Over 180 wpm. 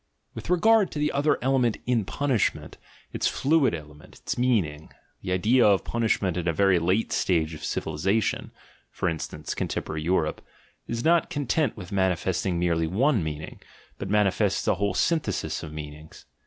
No: average, 165 wpm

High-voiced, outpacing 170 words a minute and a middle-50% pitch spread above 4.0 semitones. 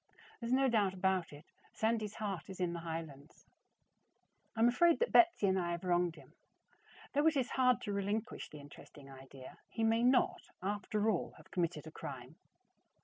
Yes: high, 195 Hz; average, 185 wpm; wide, 5.5 semitones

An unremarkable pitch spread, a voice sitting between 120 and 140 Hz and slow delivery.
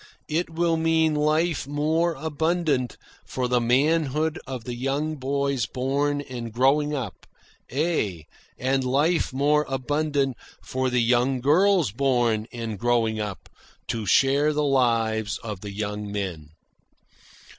Yes: average, 4.3 semitones; low, 135 Hz; slow, 130 wpm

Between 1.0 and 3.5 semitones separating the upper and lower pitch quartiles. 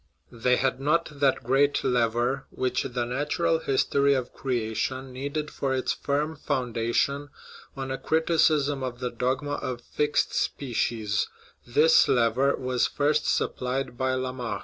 Yes: narrow, 2.6 semitones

